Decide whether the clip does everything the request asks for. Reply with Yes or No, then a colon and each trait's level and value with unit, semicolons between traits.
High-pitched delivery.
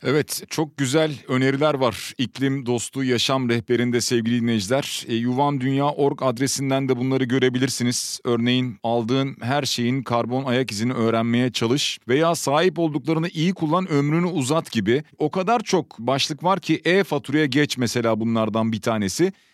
No: low, 135 Hz